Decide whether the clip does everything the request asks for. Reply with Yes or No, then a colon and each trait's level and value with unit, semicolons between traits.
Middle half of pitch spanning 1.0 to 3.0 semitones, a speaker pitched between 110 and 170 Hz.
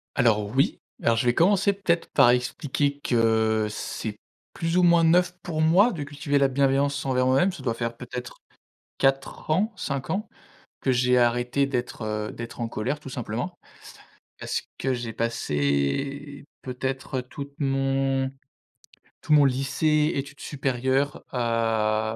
No: average, 3.4 semitones; low, 135 Hz